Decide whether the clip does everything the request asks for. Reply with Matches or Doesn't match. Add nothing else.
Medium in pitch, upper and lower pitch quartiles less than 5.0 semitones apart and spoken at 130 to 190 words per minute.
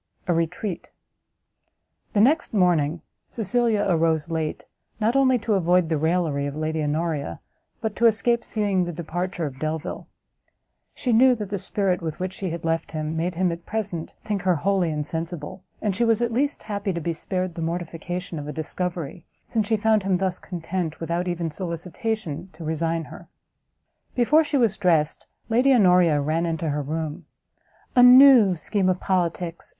Matches